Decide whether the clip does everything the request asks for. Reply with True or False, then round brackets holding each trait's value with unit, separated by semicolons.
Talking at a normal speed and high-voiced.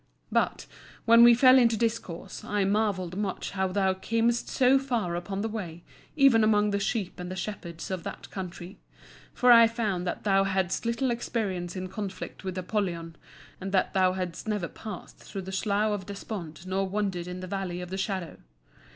True (185 wpm; 195 Hz)